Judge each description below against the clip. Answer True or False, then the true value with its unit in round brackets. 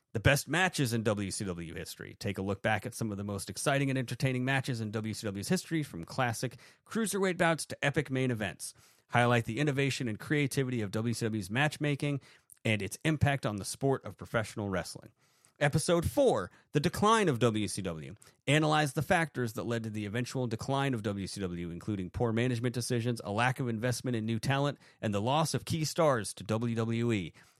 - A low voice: True (120 Hz)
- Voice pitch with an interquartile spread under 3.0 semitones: False (4.5 semitones)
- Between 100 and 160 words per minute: False (180 wpm)